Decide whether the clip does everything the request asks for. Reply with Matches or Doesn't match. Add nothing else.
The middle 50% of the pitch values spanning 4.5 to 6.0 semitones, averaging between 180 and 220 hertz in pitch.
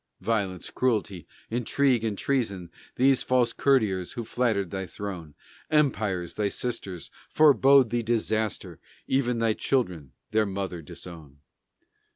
Doesn't match